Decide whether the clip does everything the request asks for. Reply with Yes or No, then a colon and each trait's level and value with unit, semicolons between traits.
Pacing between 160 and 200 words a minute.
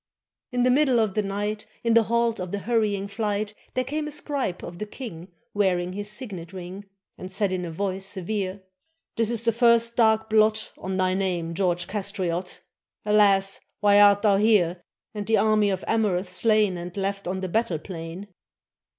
Yes: average, 185 wpm